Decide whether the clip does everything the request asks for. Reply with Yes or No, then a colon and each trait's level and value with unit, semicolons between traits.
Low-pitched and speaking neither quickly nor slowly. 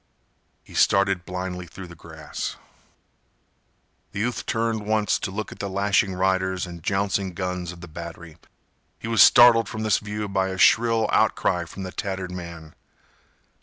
Yes: very low, 95 Hz; average, 160 wpm